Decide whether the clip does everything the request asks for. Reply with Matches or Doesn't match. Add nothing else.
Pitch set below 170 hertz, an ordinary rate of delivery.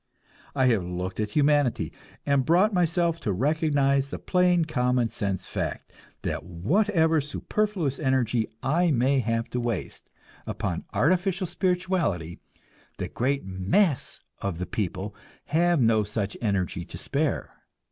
Doesn't match